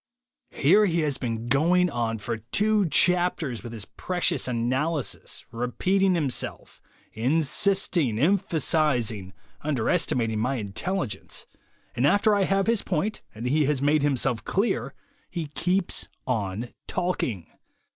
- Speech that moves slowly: Yes, slow, 120 wpm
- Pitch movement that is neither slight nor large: No, wide, 7.3 semitones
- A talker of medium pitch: Yes, medium, 145 Hz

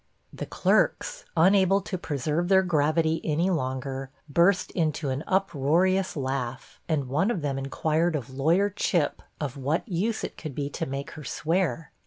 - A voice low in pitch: No, medium, 160 Hz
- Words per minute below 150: No, average, 160 wpm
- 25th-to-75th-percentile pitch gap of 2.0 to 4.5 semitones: No, average, 4.9 semitones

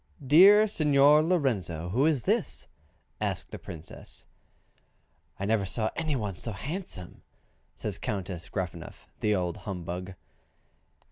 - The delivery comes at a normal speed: No, slow, 120 wpm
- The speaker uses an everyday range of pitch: No, wide, 8.5 semitones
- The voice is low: Yes, low, 105 Hz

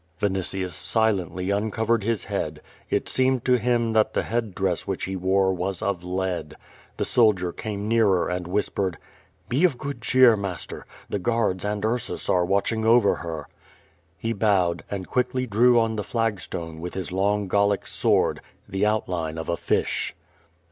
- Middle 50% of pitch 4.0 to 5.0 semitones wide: No, average, 3.6 semitones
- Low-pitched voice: Yes, low, 100 Hz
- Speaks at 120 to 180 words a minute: Yes, average, 165 wpm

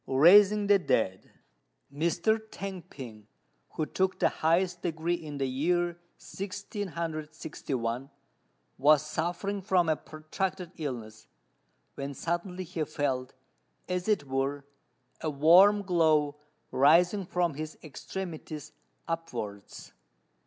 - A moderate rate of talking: No, slow, 105 wpm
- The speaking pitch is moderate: Yes, medium, 160 Hz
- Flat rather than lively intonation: No, average, 4.2 semitones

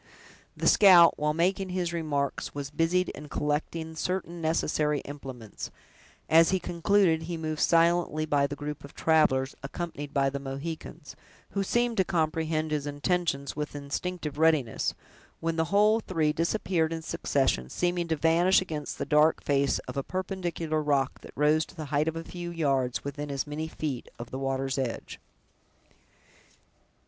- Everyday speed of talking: Yes, average, 160 wpm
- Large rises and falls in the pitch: No, average, 3.1 semitones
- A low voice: No, medium, 155 Hz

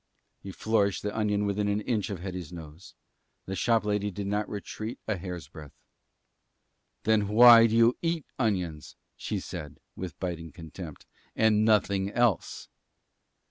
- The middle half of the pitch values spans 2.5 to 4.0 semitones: Yes, average, 3.3 semitones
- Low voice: Yes, low, 100 Hz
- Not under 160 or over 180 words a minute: No, average, 145 wpm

